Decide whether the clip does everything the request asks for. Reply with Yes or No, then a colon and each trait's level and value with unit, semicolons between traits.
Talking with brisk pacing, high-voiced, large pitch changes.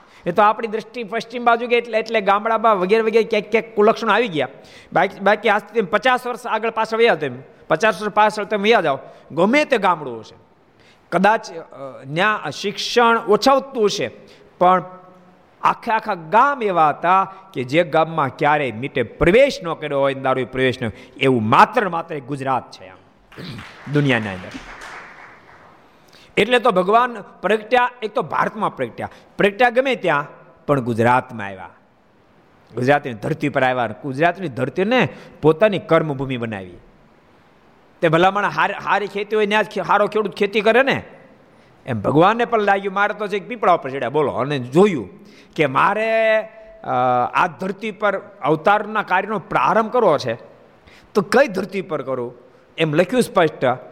Yes: fast, 150 wpm; high, 200 Hz; wide, 7.1 semitones